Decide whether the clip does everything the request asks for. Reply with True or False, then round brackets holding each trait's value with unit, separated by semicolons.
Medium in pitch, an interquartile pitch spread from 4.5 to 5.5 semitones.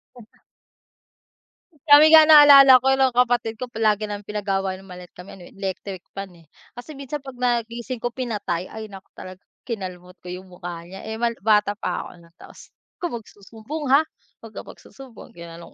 False (220 Hz; 5.1 semitones)